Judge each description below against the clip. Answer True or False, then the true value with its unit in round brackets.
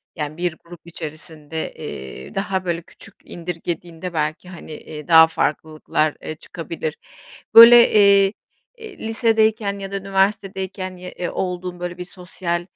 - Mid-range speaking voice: True (180 Hz)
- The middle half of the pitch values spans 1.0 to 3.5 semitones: True (3.2 semitones)